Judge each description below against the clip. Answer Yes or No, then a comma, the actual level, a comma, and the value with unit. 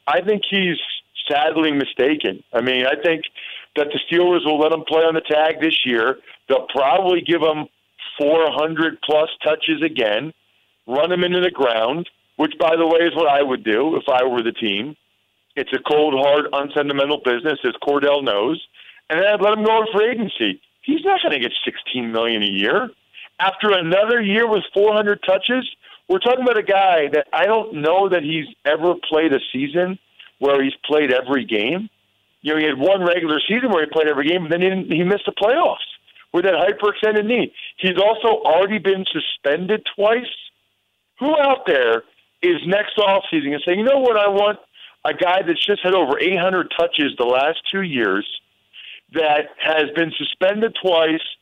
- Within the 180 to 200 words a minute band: Yes, average, 190 wpm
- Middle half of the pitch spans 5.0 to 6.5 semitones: Yes, wide, 5.6 semitones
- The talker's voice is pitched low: No, medium, 170 Hz